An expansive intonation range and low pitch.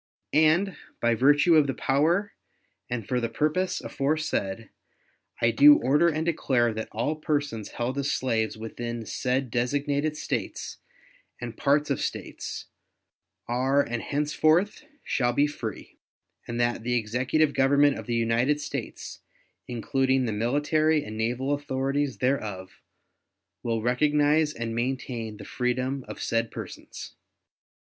No: average, 3.8 semitones; low, 130 Hz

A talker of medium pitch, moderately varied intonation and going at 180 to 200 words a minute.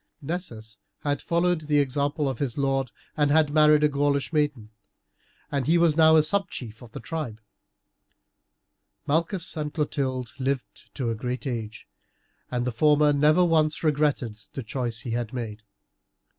No: medium, 145 Hz; average, 3.9 semitones; average, 155 wpm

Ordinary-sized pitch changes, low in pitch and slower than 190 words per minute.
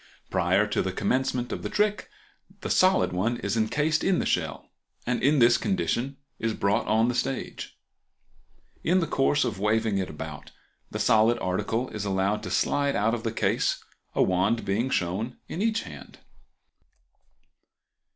Yes: average, 4.9 semitones; low, 115 Hz; average, 165 wpm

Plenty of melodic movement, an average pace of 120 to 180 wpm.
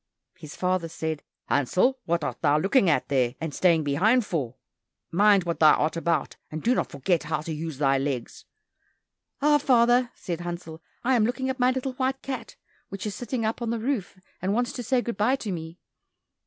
No: wide, 7.4 semitones; average, 200 wpm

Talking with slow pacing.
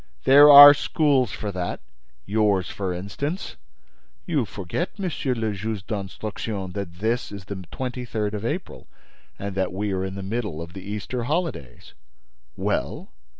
No: average, 150 wpm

